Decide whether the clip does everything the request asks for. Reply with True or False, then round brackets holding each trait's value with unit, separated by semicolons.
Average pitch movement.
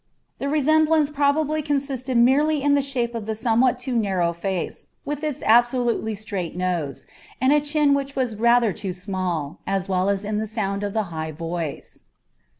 False (6.6 semitones)